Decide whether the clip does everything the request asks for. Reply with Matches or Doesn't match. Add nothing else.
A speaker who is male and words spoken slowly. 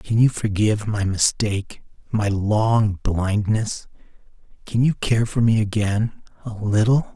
Matches